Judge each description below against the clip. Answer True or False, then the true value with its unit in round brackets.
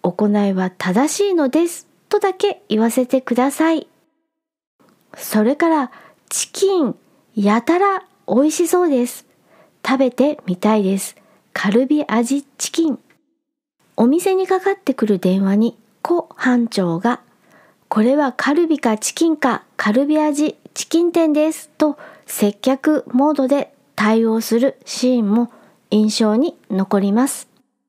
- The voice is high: True (265 Hz)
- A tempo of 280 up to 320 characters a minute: False (255 characters per minute)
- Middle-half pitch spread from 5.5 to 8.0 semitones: True (5.9 semitones)